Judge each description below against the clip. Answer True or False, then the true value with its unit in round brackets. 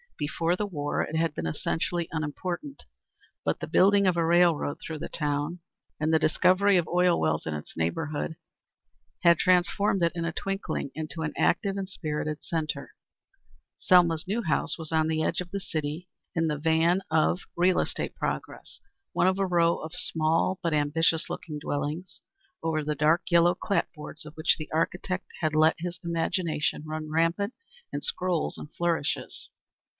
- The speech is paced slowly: False (170 wpm)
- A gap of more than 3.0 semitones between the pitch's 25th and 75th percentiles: False (2.5 semitones)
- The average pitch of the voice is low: False (165 Hz)